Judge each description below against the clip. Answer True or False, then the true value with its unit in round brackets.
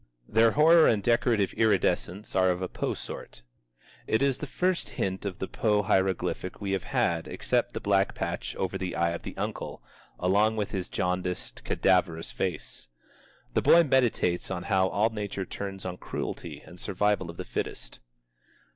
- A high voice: False (95 Hz)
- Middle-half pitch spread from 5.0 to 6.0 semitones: False (3.4 semitones)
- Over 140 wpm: True (175 wpm)